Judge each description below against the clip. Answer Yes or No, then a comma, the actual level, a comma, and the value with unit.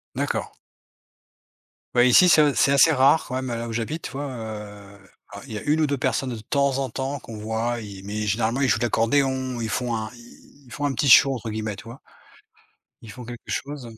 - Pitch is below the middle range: Yes, low, 125 Hz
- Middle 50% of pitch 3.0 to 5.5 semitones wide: Yes, average, 3.6 semitones